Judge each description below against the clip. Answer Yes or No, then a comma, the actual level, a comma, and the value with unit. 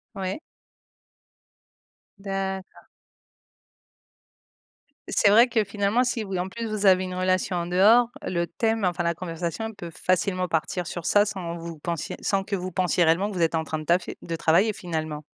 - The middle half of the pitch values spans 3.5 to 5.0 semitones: No, average, 2.9 semitones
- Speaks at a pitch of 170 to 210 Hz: Yes, medium, 185 Hz